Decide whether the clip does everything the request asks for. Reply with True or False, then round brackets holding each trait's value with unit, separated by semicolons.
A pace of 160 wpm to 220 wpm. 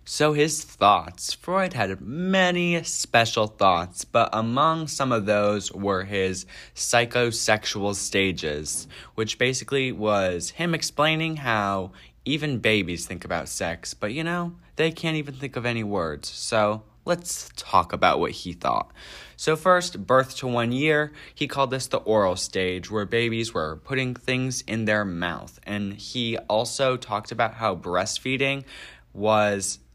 False (145 wpm)